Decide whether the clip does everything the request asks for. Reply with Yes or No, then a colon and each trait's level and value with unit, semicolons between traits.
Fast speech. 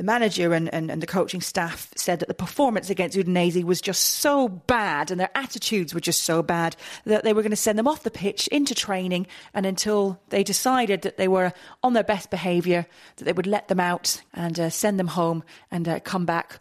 Yes: fast, 230 wpm